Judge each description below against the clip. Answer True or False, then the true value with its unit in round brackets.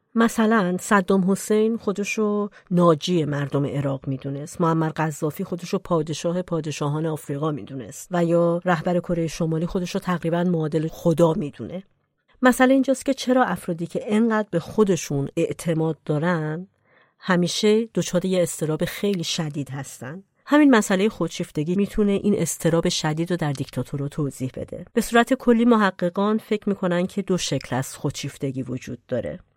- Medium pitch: True (175 Hz)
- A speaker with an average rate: True (145 wpm)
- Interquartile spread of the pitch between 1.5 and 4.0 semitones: False (4.5 semitones)